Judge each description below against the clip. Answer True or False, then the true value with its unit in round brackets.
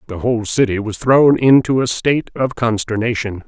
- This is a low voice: True (115 Hz)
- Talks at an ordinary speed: True (175 wpm)